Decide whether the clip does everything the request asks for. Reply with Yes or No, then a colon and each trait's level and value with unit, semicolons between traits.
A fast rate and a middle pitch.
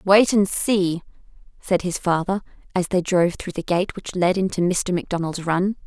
No: average, 185 wpm; medium, 180 Hz